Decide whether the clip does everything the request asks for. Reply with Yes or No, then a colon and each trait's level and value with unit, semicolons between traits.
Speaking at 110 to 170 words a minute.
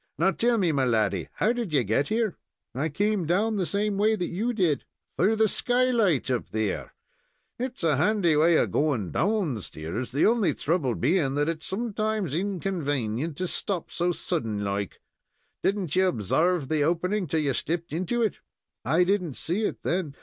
No: average, 180 wpm